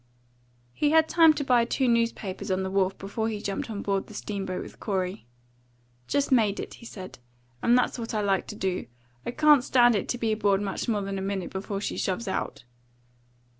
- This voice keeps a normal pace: No, fast, 210 wpm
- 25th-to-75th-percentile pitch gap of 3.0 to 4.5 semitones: Yes, average, 3.6 semitones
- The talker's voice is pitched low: No, high, 210 Hz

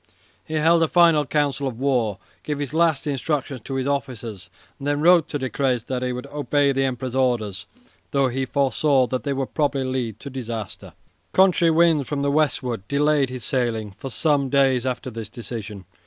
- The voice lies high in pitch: No, low, 135 Hz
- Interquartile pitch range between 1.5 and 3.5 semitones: Yes, average, 2.9 semitones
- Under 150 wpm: No, average, 185 wpm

